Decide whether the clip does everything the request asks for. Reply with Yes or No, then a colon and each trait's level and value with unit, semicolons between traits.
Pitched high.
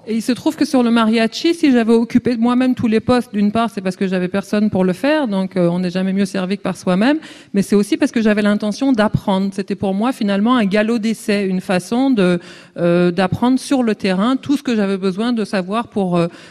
Yes: high, 210 Hz